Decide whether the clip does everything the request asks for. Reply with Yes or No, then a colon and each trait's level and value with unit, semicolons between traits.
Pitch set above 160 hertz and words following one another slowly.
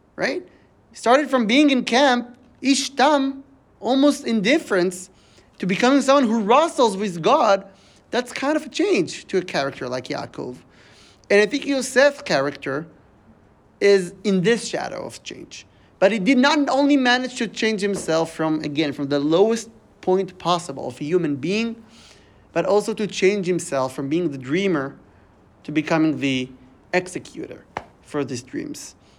No: high, 190 Hz; average, 150 wpm